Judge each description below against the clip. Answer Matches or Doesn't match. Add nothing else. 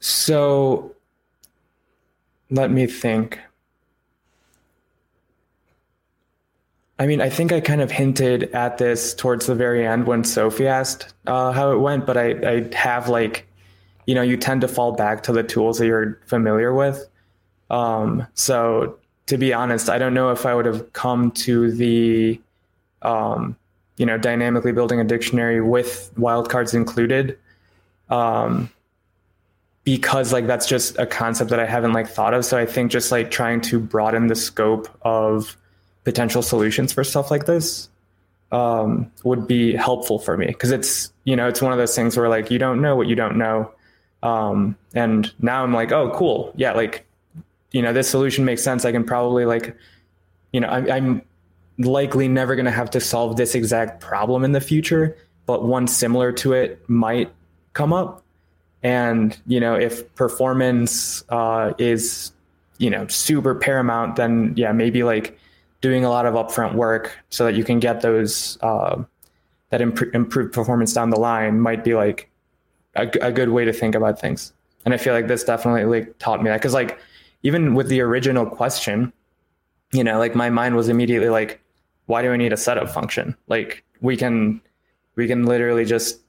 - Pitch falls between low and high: Doesn't match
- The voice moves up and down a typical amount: Doesn't match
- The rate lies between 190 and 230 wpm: Doesn't match